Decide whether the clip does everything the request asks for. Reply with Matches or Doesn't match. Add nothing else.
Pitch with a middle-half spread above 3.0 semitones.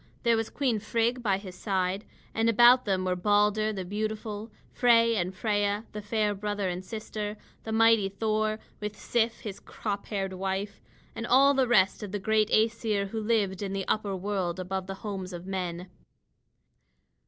Doesn't match